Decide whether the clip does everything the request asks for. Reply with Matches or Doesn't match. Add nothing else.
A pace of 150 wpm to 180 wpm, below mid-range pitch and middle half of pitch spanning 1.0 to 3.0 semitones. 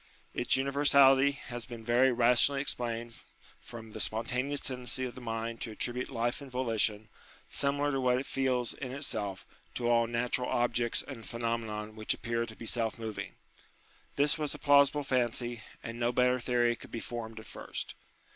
Matches